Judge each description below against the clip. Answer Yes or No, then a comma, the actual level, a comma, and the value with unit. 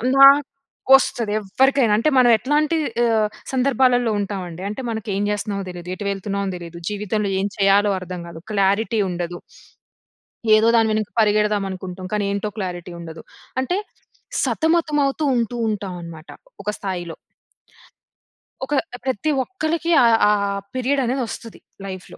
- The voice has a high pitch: Yes, high, 210 Hz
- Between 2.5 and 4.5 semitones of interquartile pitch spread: No, average, 5.3 semitones